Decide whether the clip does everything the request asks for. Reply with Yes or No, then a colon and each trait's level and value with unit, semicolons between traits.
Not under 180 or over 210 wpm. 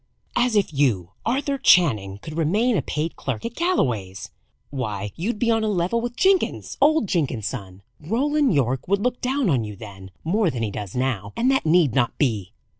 Yes: average, 190 wpm